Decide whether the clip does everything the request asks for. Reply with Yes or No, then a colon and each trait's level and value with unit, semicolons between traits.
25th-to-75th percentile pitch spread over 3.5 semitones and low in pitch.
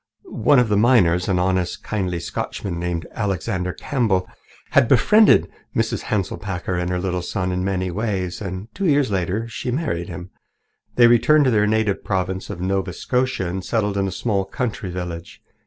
Yes: average, 3.9 semitones; very low, 95 Hz